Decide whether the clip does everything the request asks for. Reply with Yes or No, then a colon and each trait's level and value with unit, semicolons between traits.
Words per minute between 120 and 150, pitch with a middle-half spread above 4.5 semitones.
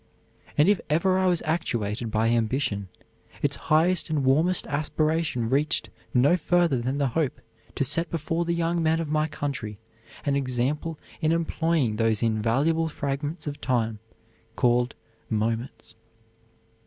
Yes: average, 140 wpm; wide, 5.4 semitones